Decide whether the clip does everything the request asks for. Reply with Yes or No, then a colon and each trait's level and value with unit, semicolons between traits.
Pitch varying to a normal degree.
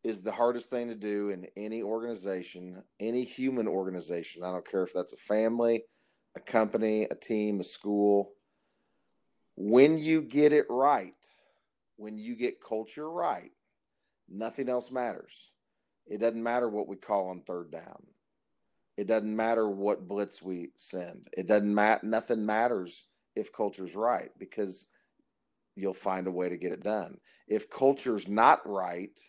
Yes: average, 3.1 semitones